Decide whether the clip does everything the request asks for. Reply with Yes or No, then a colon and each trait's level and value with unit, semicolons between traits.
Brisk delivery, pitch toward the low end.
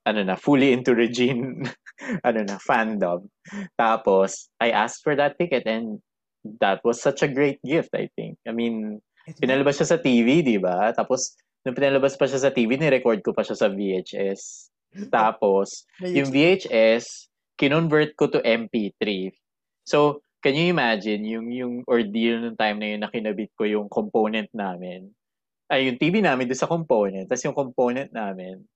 Yes: fast, 165 wpm; low, 120 Hz